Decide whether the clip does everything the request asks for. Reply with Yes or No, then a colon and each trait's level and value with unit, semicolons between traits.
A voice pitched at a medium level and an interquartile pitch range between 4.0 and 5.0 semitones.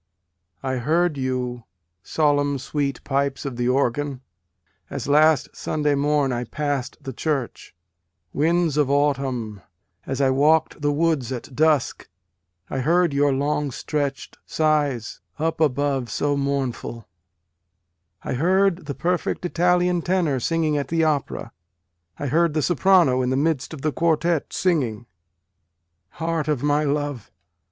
No: medium, 145 Hz; average, 3.1 semitones